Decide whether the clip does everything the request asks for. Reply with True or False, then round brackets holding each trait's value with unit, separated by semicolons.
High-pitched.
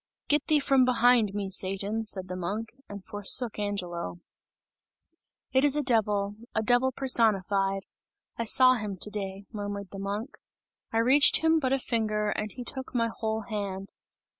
True (215 Hz)